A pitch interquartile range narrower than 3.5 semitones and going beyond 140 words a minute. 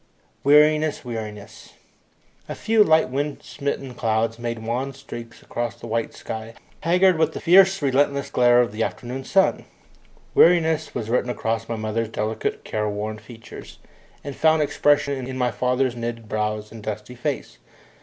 No: average, 4.4 semitones; average, 150 wpm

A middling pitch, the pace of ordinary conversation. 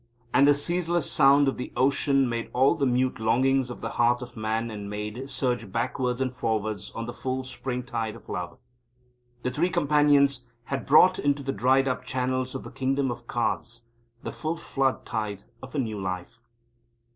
No: low, 130 Hz; average, 180 wpm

